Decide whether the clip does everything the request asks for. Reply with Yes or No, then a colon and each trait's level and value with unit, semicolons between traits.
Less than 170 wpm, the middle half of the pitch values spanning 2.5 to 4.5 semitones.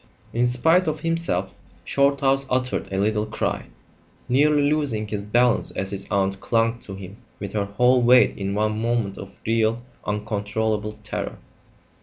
Yes: average, 150 wpm; average, 3.7 semitones